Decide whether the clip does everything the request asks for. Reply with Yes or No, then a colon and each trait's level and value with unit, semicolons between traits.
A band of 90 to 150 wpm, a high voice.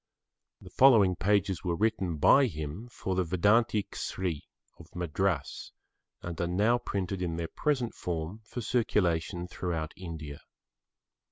No: slow, 135 wpm; very low, 95 Hz